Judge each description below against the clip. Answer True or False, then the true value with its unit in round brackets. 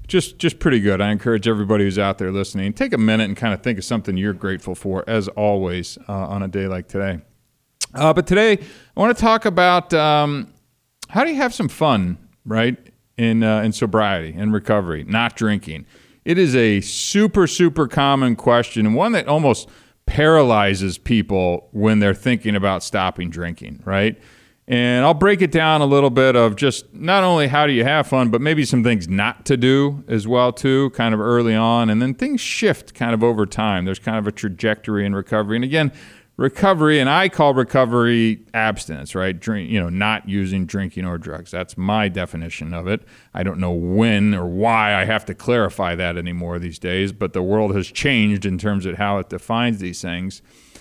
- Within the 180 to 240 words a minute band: True (200 wpm)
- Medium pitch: False (110 Hz)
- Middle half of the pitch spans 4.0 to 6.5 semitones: True (5.2 semitones)